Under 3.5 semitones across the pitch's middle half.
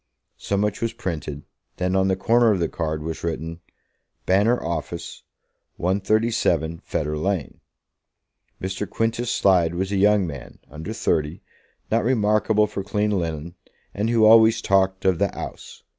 No: average, 4.3 semitones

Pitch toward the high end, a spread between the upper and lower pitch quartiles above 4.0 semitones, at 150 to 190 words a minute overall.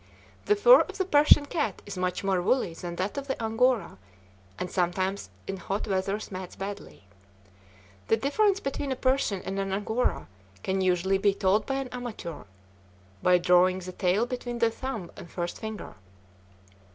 Yes: high, 200 Hz; wide, 5.4 semitones; average, 165 wpm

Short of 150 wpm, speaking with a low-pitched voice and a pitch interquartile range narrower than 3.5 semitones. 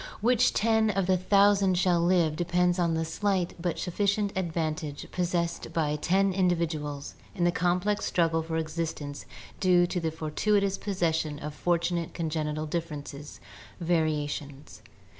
No: average, 140 wpm; medium, 170 Hz; average, 2.9 semitones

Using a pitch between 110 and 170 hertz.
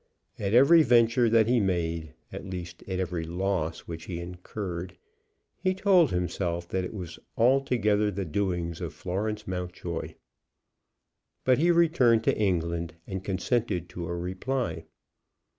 No: very low, 95 Hz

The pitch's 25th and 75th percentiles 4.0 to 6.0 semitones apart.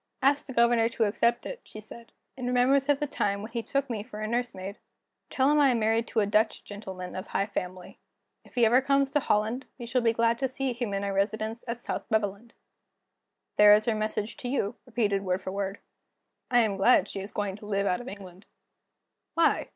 No: average, 3.4 semitones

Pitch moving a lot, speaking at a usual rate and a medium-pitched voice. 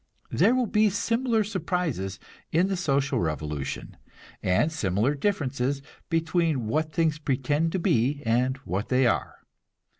No: wide, 6.5 semitones; slow, 130 wpm; medium, 145 Hz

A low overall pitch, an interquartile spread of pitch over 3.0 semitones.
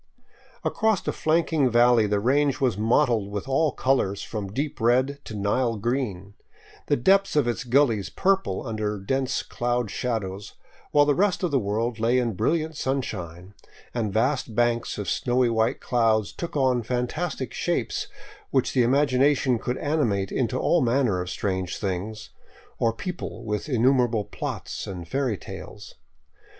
Yes: low, 120 Hz; average, 4.3 semitones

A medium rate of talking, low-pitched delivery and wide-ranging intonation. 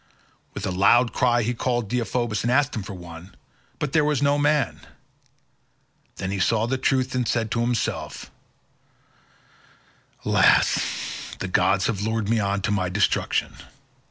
No: average, 155 wpm; low, 115 Hz; average, 4.2 semitones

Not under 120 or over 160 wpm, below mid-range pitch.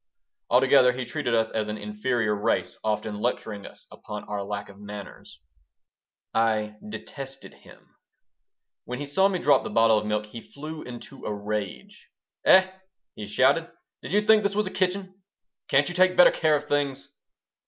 No: average, 170 wpm; low, 125 Hz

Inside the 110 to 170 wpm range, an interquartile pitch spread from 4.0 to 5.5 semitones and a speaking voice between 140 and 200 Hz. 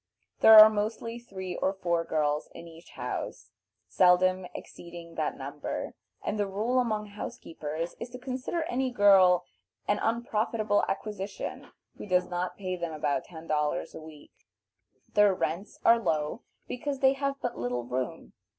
Yes: average, 155 wpm; average, 5.1 semitones; high, 190 Hz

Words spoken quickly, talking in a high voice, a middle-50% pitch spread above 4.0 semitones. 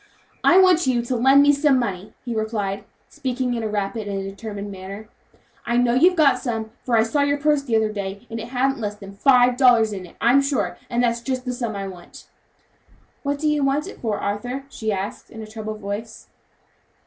Yes: fast, 215 wpm; high, 235 Hz; average, 4.5 semitones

